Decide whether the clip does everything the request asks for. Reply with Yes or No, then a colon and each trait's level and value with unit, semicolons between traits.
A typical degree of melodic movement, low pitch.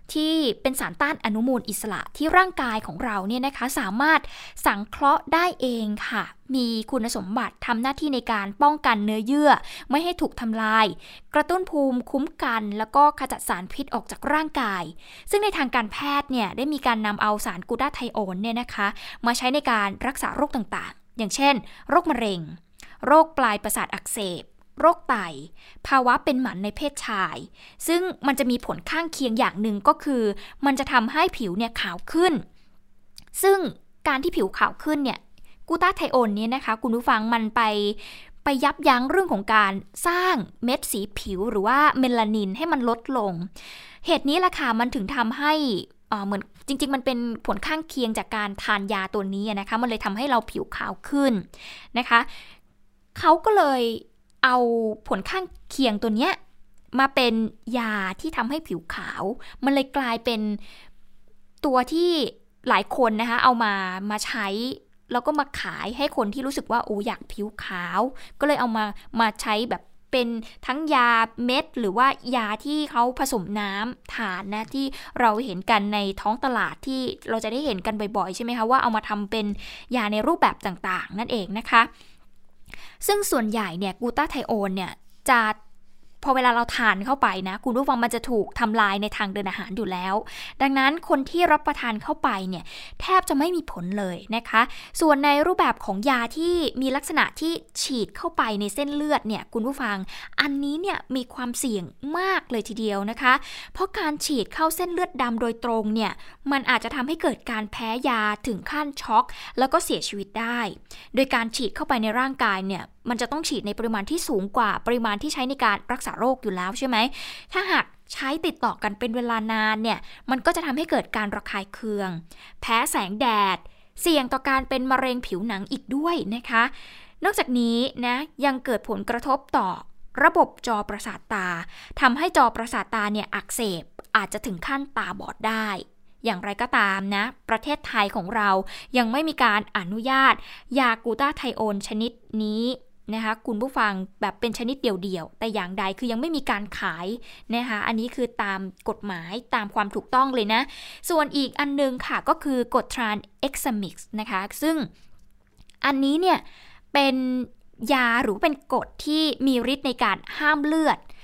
No: average, 4.7 semitones; high, 240 Hz